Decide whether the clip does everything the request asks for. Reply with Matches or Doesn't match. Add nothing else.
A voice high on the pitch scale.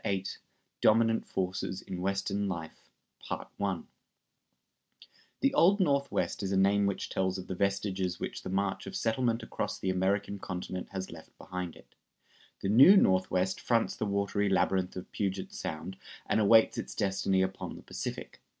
Doesn't match